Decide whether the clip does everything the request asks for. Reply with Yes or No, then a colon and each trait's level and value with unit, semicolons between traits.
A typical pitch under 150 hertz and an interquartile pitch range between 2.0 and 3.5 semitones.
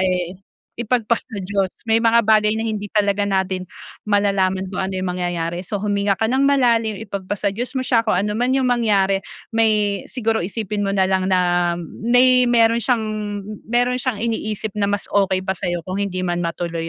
No: high, 205 Hz; average, 3.2 semitones